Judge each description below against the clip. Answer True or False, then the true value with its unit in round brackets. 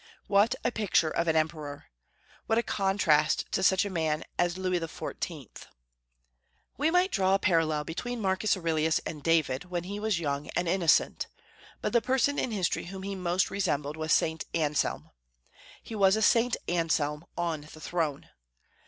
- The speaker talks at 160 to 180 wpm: True (165 wpm)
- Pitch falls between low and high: True (175 Hz)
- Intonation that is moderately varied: True (4.1 semitones)